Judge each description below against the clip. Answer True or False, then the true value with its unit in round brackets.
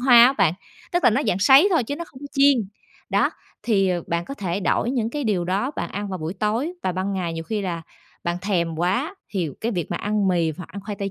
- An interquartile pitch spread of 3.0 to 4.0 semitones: False (5.4 semitones)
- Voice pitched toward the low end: False (200 Hz)